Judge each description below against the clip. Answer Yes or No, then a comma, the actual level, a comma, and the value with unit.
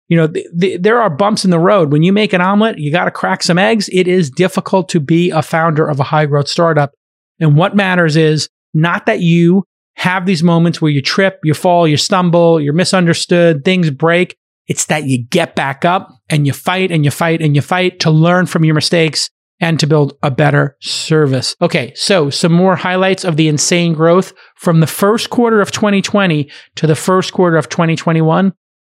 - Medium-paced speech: No, fast, 210 wpm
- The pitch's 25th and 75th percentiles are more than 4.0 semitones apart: No, average, 3.3 semitones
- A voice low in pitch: No, medium, 170 Hz